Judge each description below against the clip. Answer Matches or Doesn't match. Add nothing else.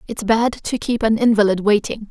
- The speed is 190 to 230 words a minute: Matches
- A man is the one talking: Doesn't match